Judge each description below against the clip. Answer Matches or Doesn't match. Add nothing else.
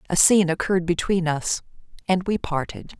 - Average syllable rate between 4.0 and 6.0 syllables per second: Matches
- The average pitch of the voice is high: Doesn't match